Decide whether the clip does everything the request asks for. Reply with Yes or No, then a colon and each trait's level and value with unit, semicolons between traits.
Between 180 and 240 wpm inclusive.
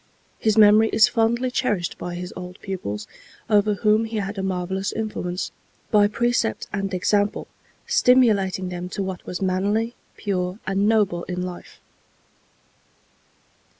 No: slow, 135 wpm